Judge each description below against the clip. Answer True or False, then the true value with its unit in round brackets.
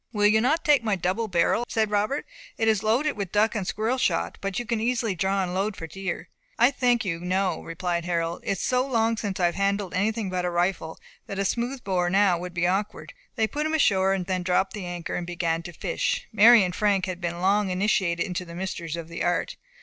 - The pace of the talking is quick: True (230 wpm)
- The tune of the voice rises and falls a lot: False (3.7 semitones)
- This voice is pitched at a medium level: False (195 Hz)